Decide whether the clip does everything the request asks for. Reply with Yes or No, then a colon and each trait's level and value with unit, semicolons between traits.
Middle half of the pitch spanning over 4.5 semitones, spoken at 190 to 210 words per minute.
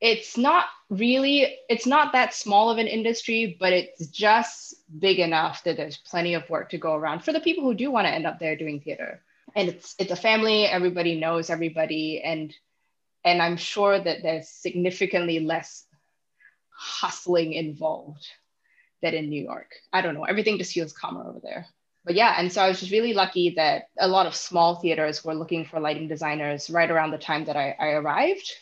Yes: average, 5.1 semitones; average, 195 wpm